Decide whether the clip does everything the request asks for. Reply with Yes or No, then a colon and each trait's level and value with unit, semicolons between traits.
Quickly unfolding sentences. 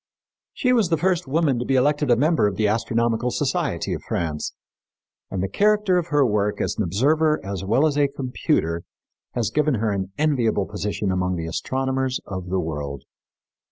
No: average, 185 wpm